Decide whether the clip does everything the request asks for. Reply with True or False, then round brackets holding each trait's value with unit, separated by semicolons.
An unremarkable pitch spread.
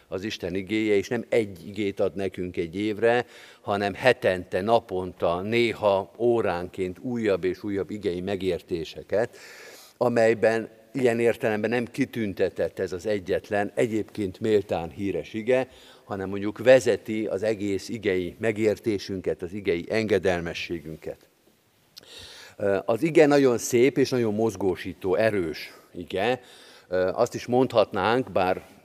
True (3.7 semitones)